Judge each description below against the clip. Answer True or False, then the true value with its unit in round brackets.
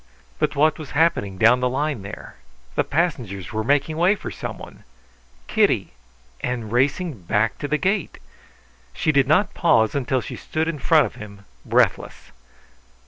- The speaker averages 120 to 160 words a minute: True (155 wpm)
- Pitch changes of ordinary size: False (6.0 semitones)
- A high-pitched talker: False (140 Hz)